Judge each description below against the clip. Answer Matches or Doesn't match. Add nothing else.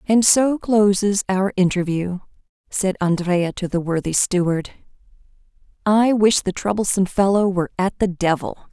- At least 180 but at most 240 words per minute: Doesn't match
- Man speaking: Doesn't match